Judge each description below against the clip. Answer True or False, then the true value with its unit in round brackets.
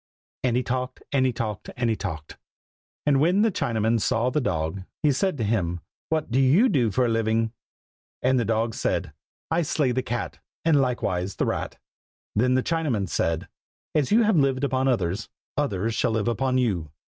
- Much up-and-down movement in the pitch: False (3.8 semitones)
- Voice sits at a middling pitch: False (125 Hz)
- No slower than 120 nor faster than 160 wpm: False (190 wpm)